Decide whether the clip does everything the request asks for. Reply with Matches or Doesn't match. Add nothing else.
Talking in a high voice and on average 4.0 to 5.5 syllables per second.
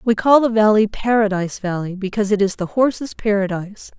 Doesn't match